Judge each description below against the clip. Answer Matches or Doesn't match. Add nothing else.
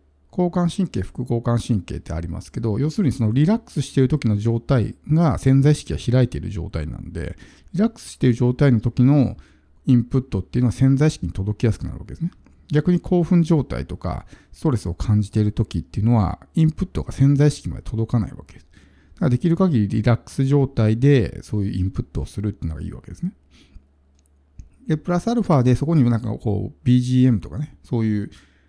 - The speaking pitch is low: Matches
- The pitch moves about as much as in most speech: Doesn't match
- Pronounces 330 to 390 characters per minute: Doesn't match